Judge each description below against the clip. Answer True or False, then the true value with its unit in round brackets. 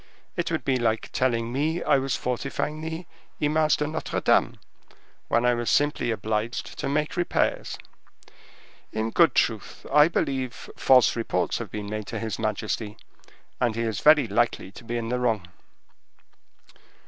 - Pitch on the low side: True (120 Hz)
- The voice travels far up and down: False (4.8 semitones)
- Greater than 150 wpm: True (160 wpm)